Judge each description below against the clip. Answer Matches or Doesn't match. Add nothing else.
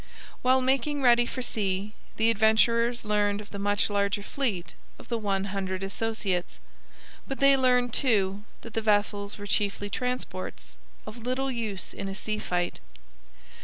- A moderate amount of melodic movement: Matches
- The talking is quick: Doesn't match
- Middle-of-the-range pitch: Doesn't match